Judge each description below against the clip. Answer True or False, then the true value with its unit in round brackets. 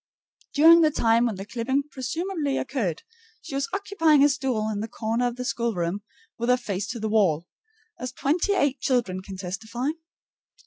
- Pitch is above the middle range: True (245 Hz)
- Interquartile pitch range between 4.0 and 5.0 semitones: True (4.6 semitones)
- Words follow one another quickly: False (175 wpm)